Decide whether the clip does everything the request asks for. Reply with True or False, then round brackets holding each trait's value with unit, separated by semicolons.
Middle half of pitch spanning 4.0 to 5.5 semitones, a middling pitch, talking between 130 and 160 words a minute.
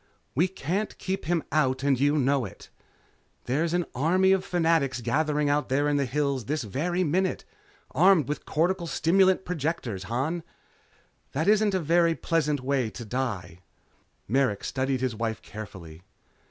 True (4.9 semitones; 145 Hz; 155 wpm)